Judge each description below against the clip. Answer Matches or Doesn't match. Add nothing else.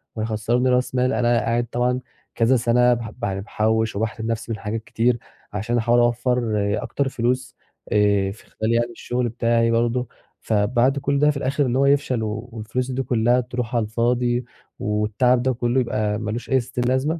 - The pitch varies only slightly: Matches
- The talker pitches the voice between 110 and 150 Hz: Matches